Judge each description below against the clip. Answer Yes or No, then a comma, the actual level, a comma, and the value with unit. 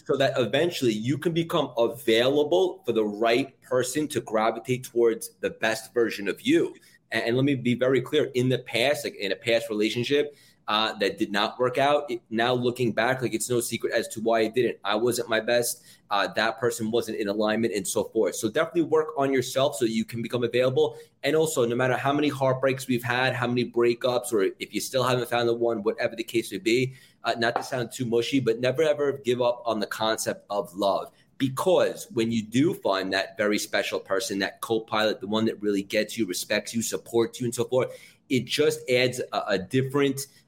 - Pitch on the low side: Yes, low, 120 Hz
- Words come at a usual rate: No, fast, 220 wpm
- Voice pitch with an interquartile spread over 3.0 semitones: Yes, average, 3.6 semitones